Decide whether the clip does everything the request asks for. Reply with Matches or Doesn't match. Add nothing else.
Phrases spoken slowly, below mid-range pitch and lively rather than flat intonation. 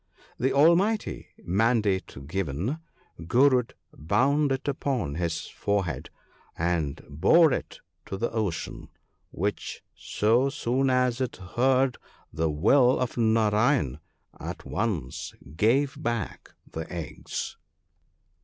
Matches